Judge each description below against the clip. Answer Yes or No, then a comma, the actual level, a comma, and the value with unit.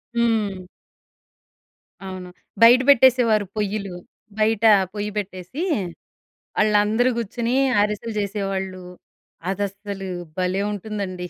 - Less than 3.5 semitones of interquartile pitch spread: Yes, average, 2.7 semitones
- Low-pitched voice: No, high, 205 Hz